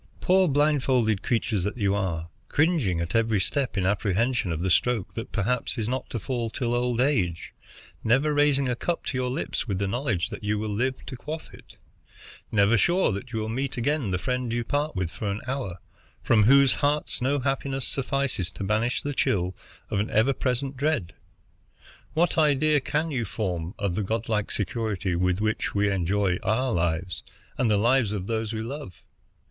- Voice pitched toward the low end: Yes, low, 115 Hz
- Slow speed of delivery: No, average, 190 wpm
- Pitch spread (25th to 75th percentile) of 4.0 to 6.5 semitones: Yes, average, 5.1 semitones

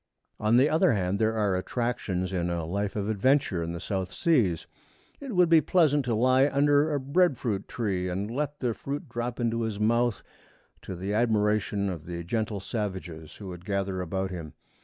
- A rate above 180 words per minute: Yes, average, 190 wpm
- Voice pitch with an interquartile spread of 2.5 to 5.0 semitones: No, wide, 5.6 semitones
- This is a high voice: No, low, 105 Hz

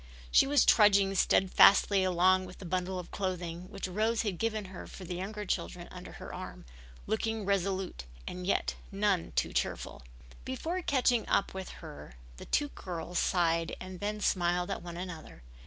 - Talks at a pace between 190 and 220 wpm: No, average, 170 wpm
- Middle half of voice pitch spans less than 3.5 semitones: Yes, average, 2.7 semitones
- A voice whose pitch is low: No, high, 190 Hz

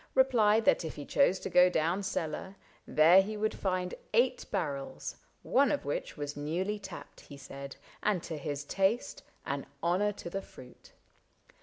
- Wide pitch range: Yes, wide, 5.8 semitones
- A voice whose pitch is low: No, medium, 180 Hz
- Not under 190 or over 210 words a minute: No, average, 170 wpm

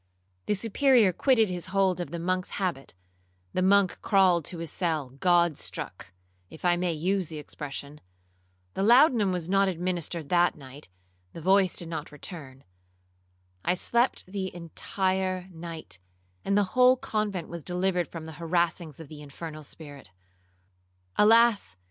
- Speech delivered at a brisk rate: No, slow, 135 wpm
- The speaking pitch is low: No, medium, 170 Hz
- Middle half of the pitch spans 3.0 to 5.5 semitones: Yes, average, 5.2 semitones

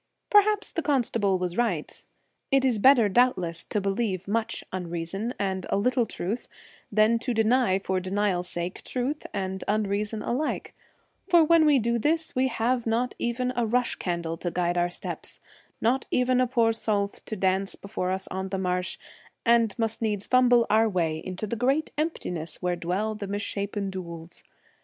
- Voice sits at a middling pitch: No, high, 215 Hz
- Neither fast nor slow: Yes, average, 175 wpm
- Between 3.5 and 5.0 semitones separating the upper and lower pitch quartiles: Yes, average, 4.7 semitones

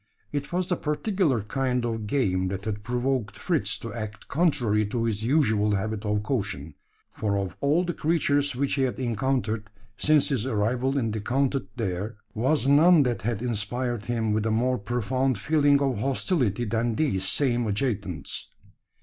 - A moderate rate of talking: Yes, average, 165 wpm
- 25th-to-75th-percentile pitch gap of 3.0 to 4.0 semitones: No, average, 4.4 semitones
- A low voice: Yes, low, 120 Hz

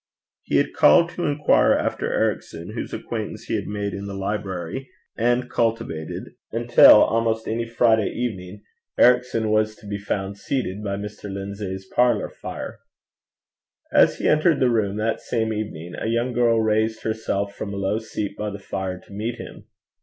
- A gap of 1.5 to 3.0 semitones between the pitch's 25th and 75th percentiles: Yes, narrow, 2.6 semitones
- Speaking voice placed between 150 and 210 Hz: No, low, 110 Hz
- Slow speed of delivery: No, average, 170 wpm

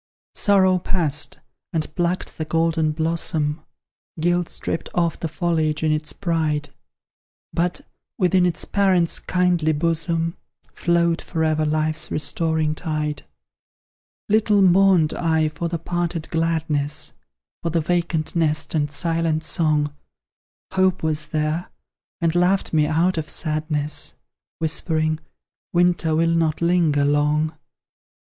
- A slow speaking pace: Yes, slow, 120 wpm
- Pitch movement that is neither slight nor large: No, narrow, 2.0 semitones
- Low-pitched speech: No, medium, 165 Hz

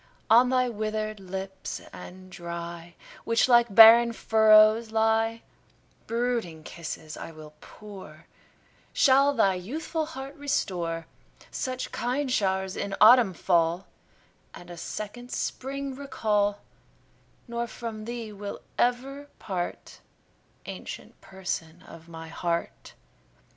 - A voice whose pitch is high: Yes, high, 215 Hz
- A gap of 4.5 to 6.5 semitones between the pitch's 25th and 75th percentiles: Yes, average, 5.1 semitones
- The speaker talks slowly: Yes, slow, 110 wpm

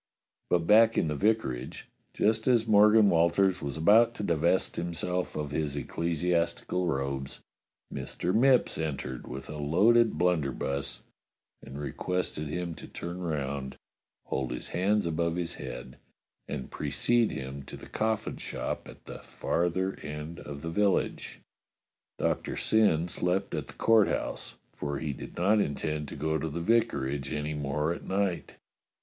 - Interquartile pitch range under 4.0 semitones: No, average, 5.2 semitones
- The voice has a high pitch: No, very low, 85 Hz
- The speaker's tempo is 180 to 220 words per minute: No, average, 150 wpm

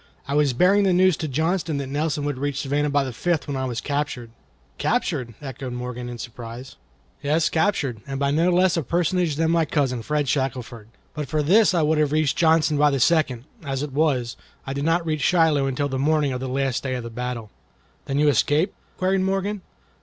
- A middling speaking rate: No, fast, 215 wpm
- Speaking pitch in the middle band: Yes, medium, 145 Hz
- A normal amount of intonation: Yes, average, 3.6 semitones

